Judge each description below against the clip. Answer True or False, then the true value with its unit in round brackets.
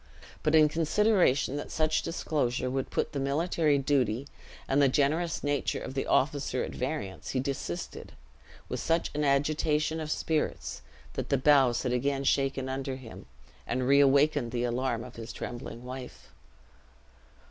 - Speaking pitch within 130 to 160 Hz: True (140 Hz)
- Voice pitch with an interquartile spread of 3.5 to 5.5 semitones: False (2.8 semitones)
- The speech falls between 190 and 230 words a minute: False (150 wpm)